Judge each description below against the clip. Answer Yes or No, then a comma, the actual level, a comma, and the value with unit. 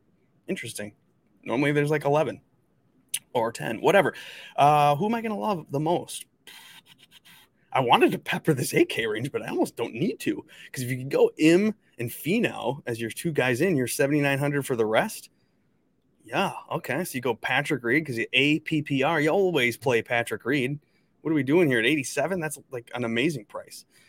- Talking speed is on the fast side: No, average, 185 wpm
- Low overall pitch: No, medium, 145 Hz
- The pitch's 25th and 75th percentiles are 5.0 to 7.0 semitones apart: Yes, wide, 5.5 semitones